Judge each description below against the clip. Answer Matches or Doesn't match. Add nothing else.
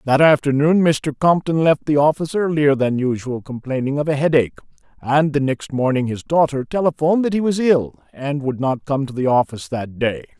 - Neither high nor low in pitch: Matches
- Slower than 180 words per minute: Doesn't match